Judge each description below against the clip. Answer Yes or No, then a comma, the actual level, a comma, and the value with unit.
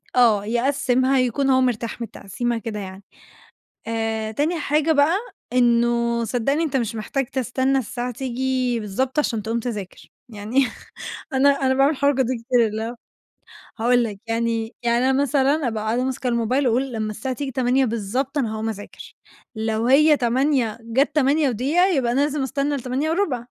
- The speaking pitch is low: No, very high, 250 Hz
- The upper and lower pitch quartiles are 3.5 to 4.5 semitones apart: No, average, 3.0 semitones